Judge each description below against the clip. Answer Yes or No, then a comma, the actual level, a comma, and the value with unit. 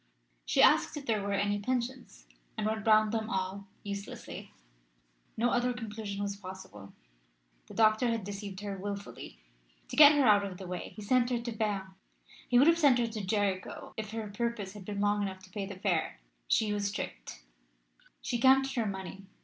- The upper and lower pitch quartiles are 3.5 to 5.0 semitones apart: No, average, 2.8 semitones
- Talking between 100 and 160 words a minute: No, average, 190 wpm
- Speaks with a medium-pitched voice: No, high, 205 Hz